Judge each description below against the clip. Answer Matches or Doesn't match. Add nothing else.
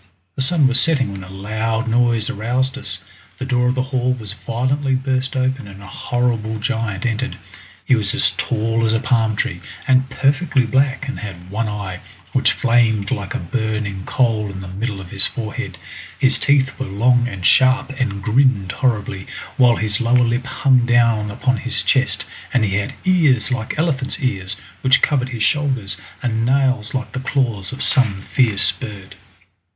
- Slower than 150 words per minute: Doesn't match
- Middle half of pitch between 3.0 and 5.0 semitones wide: Matches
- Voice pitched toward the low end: Matches